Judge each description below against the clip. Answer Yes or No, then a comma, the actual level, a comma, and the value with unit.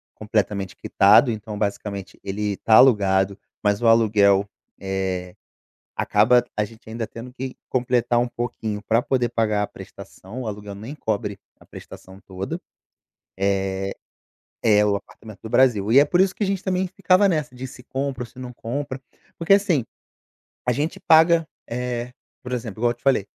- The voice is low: Yes, low, 115 Hz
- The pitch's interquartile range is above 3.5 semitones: Yes, average, 4.1 semitones